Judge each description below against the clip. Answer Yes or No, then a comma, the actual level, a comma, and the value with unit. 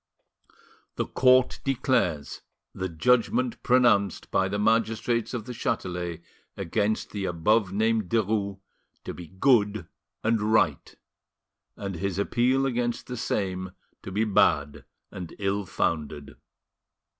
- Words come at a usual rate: No, slow, 120 wpm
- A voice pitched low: Yes, low, 105 Hz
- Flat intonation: No, average, 4.1 semitones